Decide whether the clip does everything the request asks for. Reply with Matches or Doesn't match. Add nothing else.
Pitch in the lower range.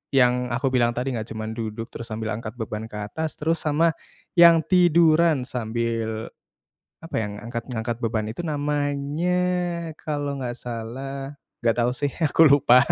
Matches